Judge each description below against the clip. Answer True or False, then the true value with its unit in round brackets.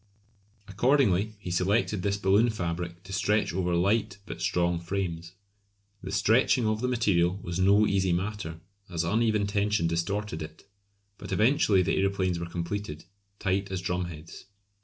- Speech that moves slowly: False (145 wpm)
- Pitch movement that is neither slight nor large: True (3.2 semitones)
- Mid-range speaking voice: False (95 Hz)